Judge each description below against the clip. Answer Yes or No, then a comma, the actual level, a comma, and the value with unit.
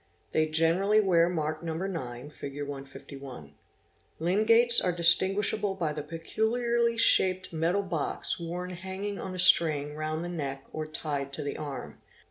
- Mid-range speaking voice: Yes, medium, 165 Hz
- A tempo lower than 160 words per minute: Yes, average, 150 wpm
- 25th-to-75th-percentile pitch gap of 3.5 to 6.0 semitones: Yes, average, 4.1 semitones